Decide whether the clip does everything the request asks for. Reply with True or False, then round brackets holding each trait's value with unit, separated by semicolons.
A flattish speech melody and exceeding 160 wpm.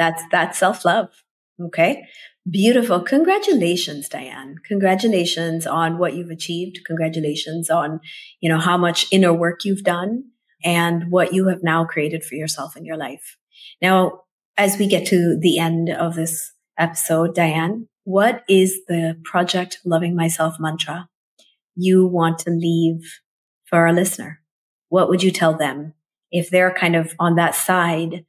False (2.1 semitones; 150 wpm)